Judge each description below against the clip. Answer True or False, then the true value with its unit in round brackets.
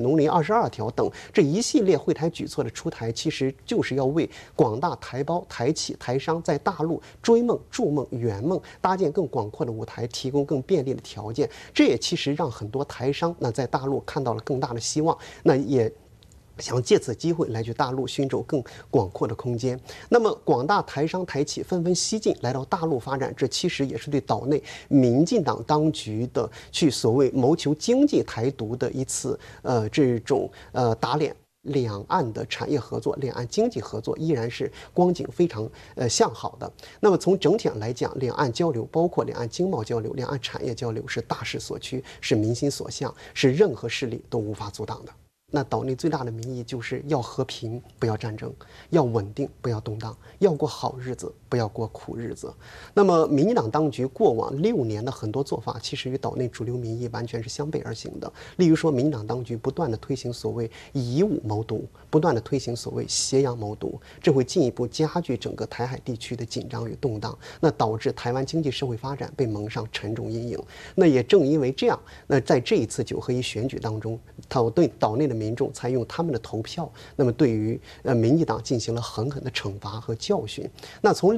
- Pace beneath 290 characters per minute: False (300 characters per minute)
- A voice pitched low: True (130 Hz)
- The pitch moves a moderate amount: True (4.6 semitones)